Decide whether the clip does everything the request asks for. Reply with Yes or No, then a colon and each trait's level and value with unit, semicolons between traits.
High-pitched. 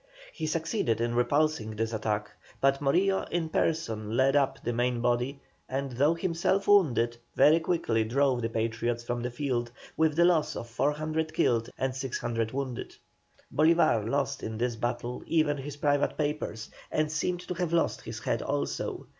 No: low, 135 Hz